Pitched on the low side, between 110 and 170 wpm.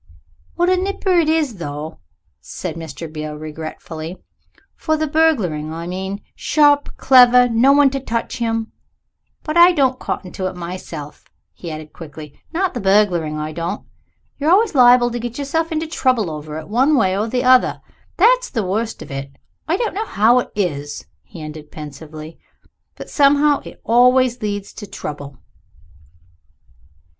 No: high, 220 Hz; average, 160 wpm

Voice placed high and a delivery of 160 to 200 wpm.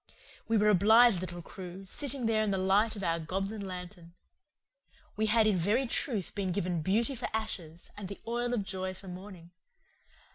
Yes: high, 195 Hz; average, 185 wpm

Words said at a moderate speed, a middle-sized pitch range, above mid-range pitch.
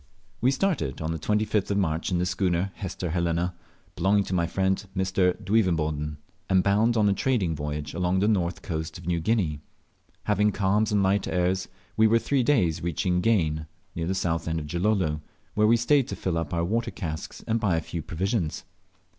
No: average, 195 wpm; average, 4.2 semitones; very low, 90 Hz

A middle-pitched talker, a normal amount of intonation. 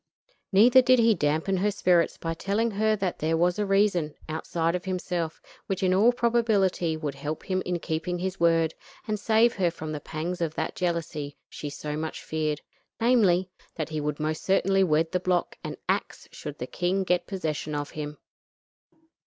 Yes: medium, 175 Hz; average, 3.7 semitones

